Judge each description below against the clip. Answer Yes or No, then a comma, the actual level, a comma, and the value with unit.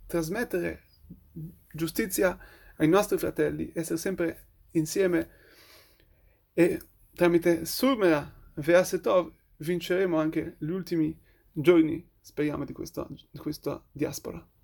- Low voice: No, medium, 165 Hz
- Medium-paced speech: No, slow, 95 wpm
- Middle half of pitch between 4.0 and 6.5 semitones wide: No, average, 3.0 semitones